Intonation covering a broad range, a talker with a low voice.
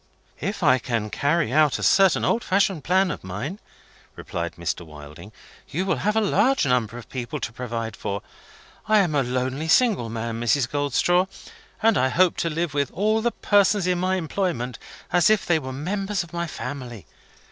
No: wide, 7.8 semitones; medium, 150 Hz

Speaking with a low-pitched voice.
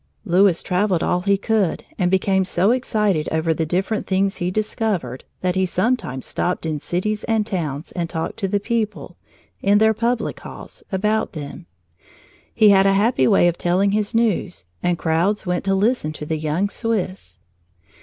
No: high, 190 Hz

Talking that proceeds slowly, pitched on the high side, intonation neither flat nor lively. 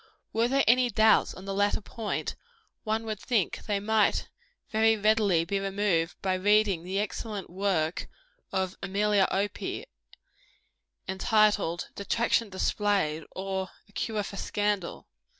No: slow, 130 wpm; high, 205 Hz; narrow, 2.3 semitones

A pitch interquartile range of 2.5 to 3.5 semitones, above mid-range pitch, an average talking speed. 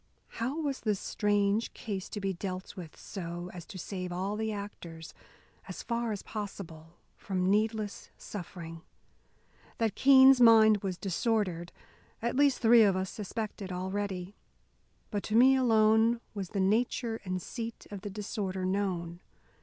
Yes: average, 3.2 semitones; high, 205 Hz; average, 145 wpm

